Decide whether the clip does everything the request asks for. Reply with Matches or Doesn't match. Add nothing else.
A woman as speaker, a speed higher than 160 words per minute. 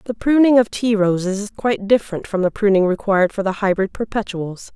Matches